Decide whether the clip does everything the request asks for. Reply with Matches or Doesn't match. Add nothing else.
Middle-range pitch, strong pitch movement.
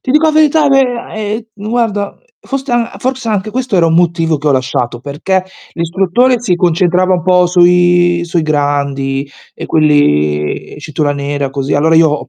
Matches